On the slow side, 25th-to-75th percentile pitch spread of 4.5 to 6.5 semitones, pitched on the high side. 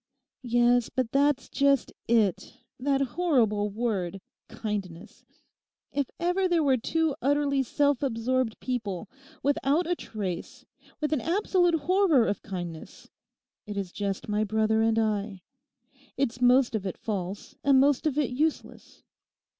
Yes: slow, 130 wpm; average, 5.3 semitones; high, 245 Hz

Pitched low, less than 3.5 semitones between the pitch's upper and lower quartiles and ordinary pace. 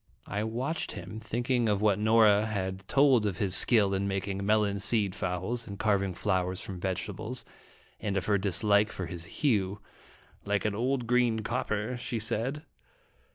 Yes: low, 105 Hz; average, 2.8 semitones; average, 160 wpm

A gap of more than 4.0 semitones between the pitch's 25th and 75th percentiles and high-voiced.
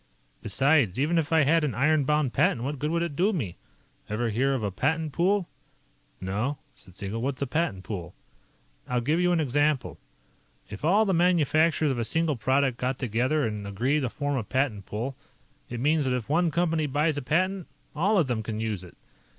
No: average, 5.3 semitones; medium, 140 Hz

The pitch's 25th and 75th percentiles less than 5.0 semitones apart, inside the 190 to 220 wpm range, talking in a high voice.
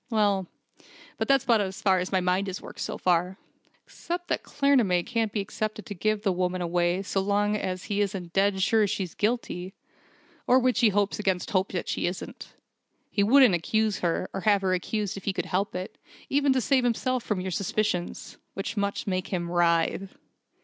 Yes: average, 2.8 semitones; average, 195 wpm; high, 195 Hz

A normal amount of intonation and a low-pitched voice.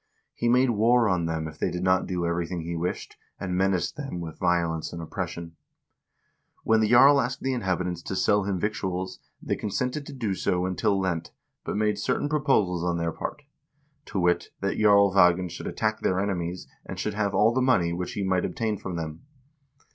Yes: average, 4.0 semitones; very low, 95 Hz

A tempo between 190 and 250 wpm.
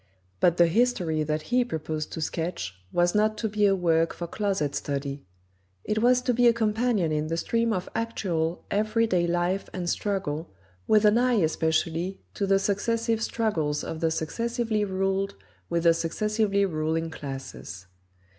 No: average, 165 wpm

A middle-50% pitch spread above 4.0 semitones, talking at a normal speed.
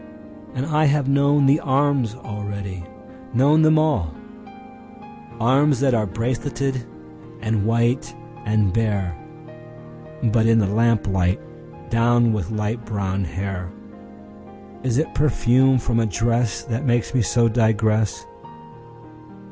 No: average, 4.5 semitones; slow, 105 wpm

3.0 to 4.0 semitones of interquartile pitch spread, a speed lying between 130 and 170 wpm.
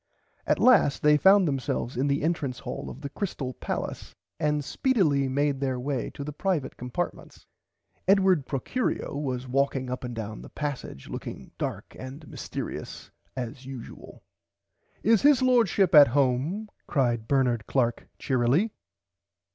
No: average, 5.1 semitones; average, 140 wpm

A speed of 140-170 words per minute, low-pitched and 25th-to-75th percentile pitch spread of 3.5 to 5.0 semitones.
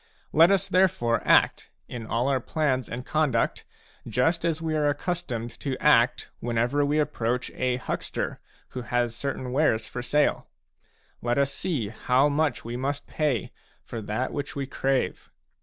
Yes: average, 155 wpm; low, 130 Hz; average, 3.8 semitones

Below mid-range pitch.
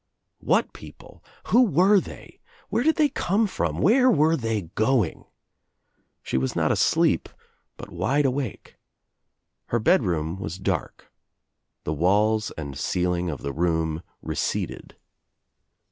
Yes: low, 110 Hz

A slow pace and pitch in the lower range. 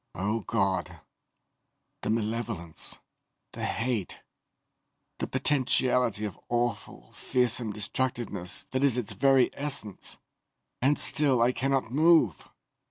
Yes: slow, 100 wpm; low, 120 Hz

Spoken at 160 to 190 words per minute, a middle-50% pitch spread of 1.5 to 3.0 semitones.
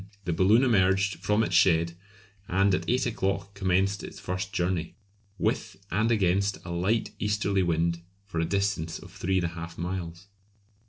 Yes: average, 165 wpm; narrow, 2.6 semitones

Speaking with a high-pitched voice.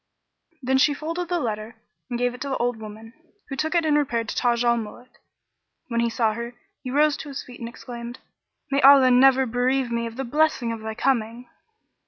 Yes: high, 245 Hz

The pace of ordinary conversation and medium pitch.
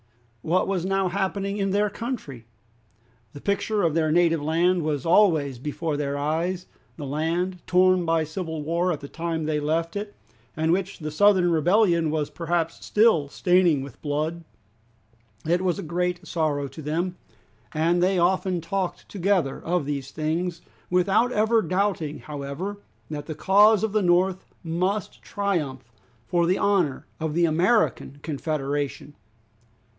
Yes: average, 150 wpm; medium, 170 Hz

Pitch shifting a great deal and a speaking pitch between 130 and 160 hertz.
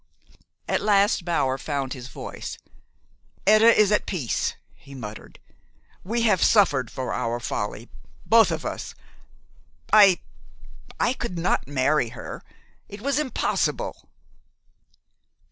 No: wide, 8.6 semitones; medium, 175 Hz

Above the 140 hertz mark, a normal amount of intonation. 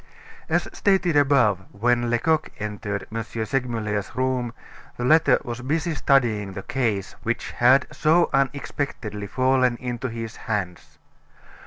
No: low, 120 Hz; average, 4.1 semitones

